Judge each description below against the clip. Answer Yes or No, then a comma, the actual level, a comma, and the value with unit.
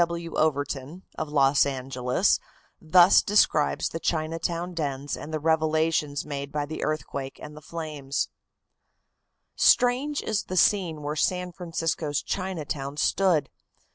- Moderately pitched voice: Yes, medium, 155 Hz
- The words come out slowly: Yes, slow, 130 wpm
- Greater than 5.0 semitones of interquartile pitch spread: No, average, 3.0 semitones